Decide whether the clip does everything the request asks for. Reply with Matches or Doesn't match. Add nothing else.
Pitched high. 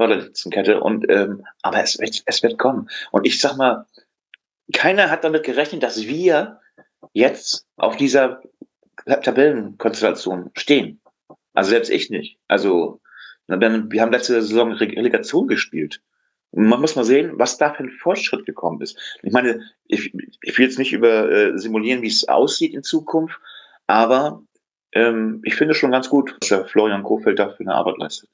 Doesn't match